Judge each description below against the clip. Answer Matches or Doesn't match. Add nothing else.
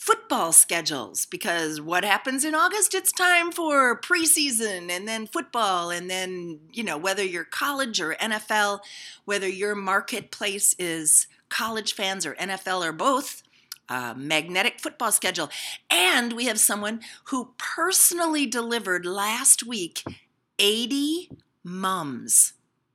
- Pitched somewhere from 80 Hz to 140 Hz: Doesn't match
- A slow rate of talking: Matches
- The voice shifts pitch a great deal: Matches